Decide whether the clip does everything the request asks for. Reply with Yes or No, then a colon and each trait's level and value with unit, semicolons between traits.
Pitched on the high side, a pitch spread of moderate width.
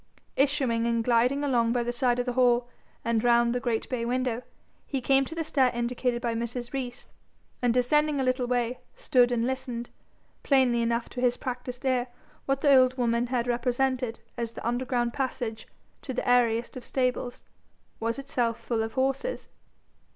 No: high, 245 Hz; narrow, 1.7 semitones